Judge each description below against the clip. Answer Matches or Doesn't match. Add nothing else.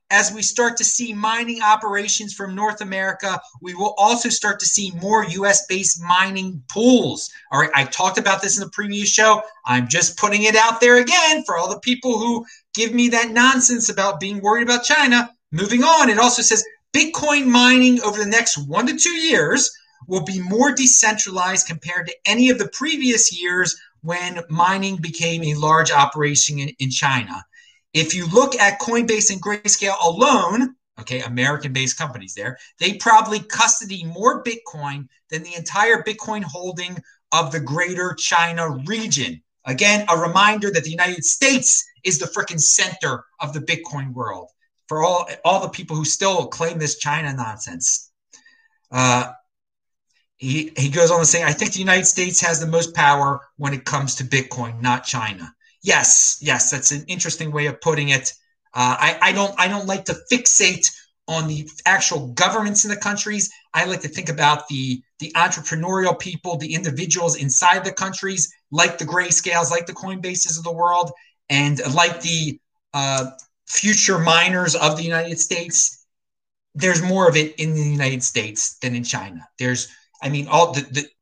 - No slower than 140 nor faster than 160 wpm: Doesn't match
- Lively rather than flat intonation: Matches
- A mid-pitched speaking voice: Matches